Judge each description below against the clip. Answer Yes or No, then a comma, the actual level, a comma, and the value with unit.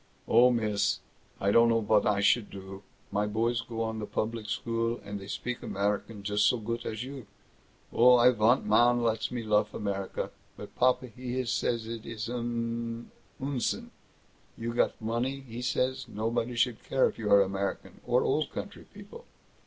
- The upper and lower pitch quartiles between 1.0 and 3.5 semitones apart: Yes, narrow, 2.5 semitones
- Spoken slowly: No, average, 175 wpm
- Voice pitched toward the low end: Yes, low, 115 Hz